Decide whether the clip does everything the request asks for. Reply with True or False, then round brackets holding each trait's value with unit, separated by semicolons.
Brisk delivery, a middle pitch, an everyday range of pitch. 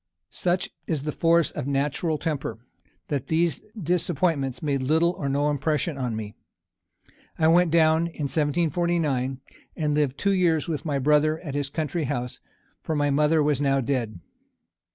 False (155 wpm; 150 Hz; 3.0 semitones)